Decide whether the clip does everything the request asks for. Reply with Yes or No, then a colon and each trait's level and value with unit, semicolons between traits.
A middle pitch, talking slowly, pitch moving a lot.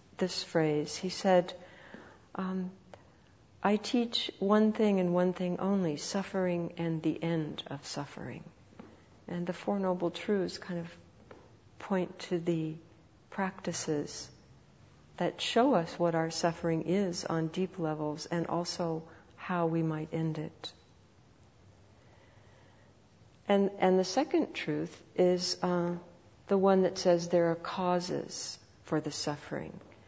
No: medium, 170 Hz; slow, 130 wpm; average, 3.0 semitones